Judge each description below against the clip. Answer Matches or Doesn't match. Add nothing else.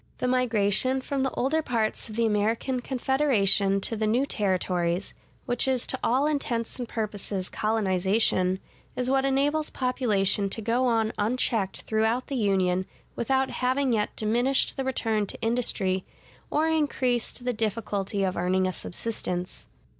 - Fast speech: Doesn't match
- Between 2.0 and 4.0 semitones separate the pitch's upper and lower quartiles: Doesn't match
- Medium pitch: Doesn't match